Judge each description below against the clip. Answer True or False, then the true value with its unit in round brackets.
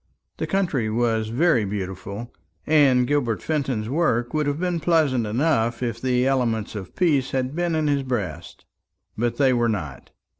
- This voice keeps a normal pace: True (160 wpm)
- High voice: False (125 Hz)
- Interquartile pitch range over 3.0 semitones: True (4.6 semitones)